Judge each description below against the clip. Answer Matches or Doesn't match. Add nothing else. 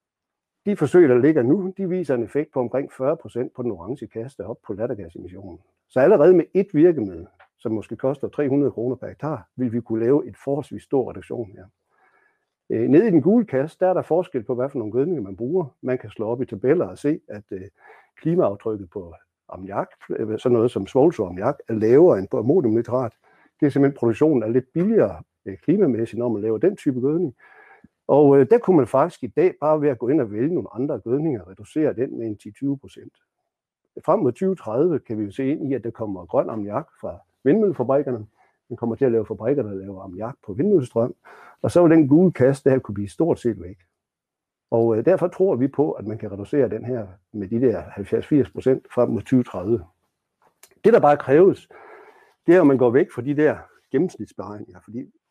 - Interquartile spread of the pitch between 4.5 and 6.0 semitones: Matches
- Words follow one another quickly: Doesn't match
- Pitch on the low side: Matches